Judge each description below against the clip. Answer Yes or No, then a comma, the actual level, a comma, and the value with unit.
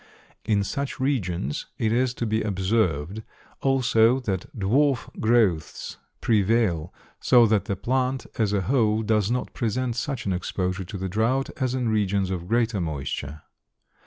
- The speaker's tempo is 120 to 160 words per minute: Yes, average, 150 wpm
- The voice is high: No, low, 110 Hz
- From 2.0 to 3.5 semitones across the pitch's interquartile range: No, average, 4.3 semitones